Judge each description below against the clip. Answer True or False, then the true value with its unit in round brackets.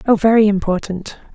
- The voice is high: True (205 Hz)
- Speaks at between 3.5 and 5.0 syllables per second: False (5.6 syllables/s)